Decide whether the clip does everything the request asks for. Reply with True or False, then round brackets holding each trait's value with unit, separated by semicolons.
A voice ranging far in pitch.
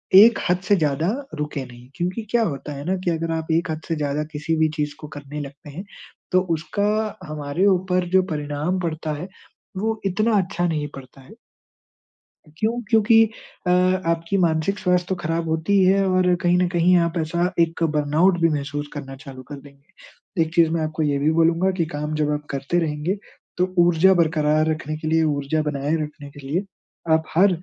False (3.5 semitones)